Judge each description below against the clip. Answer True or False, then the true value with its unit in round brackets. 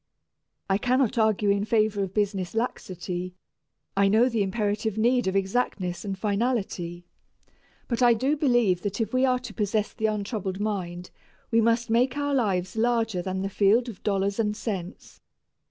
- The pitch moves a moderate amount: True (3.4 semitones)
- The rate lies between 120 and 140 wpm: False (165 wpm)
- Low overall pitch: False (210 Hz)